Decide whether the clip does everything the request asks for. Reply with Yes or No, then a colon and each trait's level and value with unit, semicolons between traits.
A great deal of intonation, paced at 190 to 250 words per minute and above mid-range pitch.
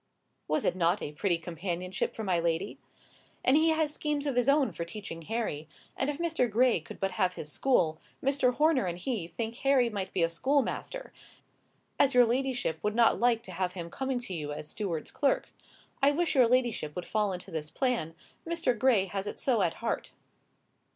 Yes: wide, 7.2 semitones; average, 195 wpm; high, 220 Hz